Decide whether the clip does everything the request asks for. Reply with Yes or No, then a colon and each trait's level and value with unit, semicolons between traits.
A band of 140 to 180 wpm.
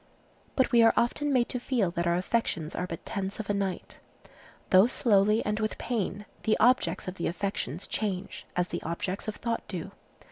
No: average, 190 wpm